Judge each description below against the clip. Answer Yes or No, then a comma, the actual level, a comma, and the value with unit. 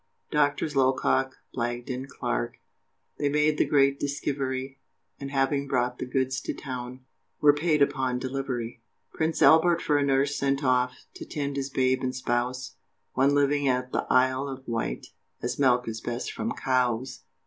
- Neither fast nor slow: Yes, average, 160 wpm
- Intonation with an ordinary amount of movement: No, narrow, 1.8 semitones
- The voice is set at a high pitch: No, low, 135 Hz